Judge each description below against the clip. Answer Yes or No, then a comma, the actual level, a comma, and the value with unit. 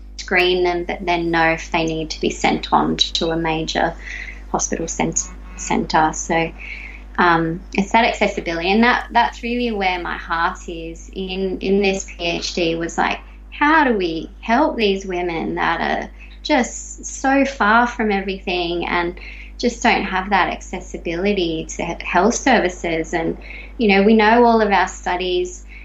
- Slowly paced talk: No, average, 160 wpm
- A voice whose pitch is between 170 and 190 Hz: Yes, medium, 185 Hz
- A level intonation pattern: No, average, 4.4 semitones